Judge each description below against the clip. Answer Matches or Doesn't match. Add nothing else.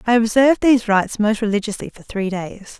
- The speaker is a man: Doesn't match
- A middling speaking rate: Matches